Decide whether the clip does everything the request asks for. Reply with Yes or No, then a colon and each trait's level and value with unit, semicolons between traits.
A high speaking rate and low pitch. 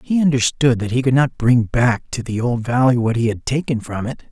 Yes: fast, 250 wpm; low, 125 Hz